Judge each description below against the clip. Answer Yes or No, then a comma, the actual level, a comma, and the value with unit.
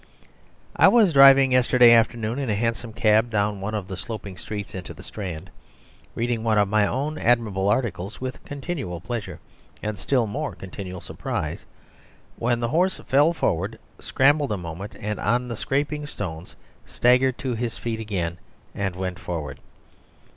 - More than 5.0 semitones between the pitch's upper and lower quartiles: No, average, 4.6 semitones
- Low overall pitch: Yes, low, 110 Hz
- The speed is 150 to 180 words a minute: Yes, average, 155 wpm